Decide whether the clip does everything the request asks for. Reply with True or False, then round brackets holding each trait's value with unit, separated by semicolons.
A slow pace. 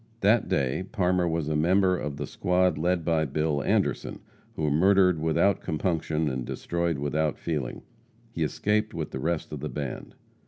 False (165 wpm)